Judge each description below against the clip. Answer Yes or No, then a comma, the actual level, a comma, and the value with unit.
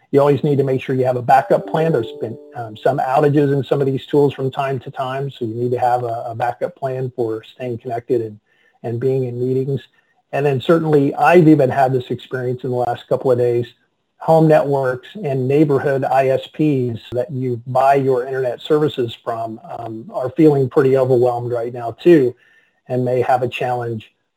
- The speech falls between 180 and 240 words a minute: Yes, average, 200 wpm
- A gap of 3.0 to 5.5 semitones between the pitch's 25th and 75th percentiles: No, narrow, 2.5 semitones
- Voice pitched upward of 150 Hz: No, low, 130 Hz